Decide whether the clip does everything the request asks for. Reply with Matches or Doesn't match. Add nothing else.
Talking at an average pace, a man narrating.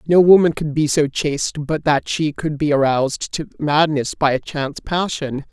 Matches